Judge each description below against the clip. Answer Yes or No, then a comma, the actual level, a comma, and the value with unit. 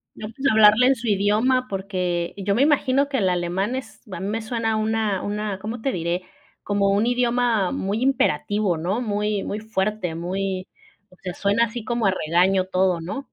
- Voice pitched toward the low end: No, high, 210 Hz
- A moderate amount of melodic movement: Yes, average, 3.4 semitones